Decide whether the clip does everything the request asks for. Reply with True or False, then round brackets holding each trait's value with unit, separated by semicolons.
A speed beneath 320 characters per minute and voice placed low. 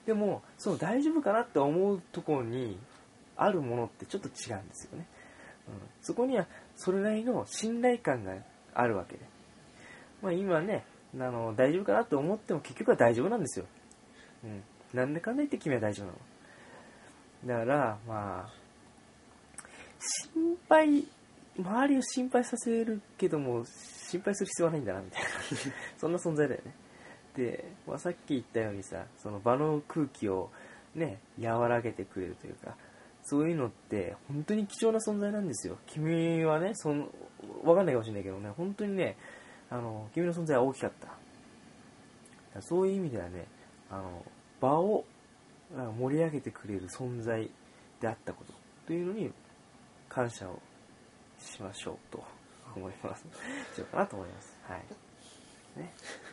False (305 characters per minute; 150 Hz)